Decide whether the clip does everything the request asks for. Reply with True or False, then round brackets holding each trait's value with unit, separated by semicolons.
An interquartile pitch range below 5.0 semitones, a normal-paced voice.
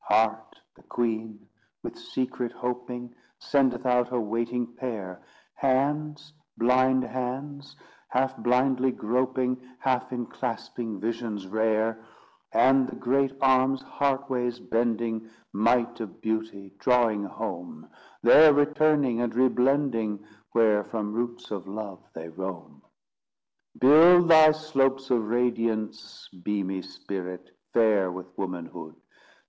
False (3.3 semitones; 110 wpm)